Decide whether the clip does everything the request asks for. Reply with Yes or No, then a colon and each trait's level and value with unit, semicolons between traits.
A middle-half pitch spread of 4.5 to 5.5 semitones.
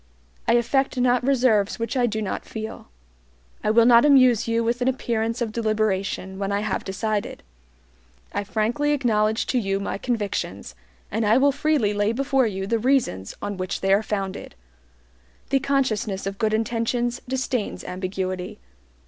No: average, 3.4 semitones